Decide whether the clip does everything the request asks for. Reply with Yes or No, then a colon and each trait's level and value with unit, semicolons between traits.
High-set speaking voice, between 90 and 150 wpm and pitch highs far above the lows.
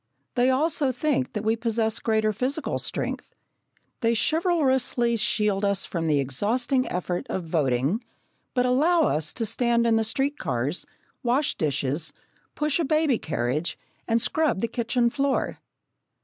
Yes: high, 230 Hz; average, 145 wpm; wide, 5.8 semitones